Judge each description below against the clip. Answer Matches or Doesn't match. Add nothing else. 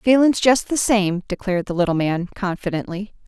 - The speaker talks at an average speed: Matches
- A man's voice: Doesn't match